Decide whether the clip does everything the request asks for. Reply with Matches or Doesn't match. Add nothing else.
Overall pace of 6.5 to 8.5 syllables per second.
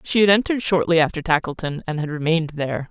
Matches